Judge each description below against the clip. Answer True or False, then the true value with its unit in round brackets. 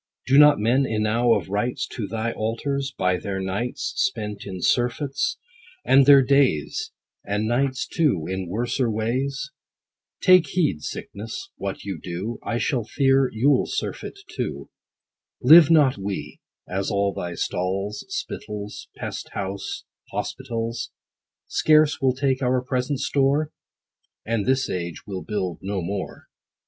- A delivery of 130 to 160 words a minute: True (135 wpm)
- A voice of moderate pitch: False (115 Hz)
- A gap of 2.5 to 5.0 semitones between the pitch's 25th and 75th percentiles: False (5.4 semitones)